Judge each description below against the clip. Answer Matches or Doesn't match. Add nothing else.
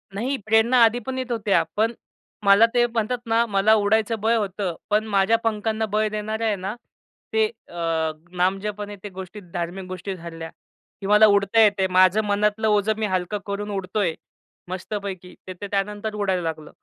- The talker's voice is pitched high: Matches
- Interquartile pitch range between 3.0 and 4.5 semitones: Doesn't match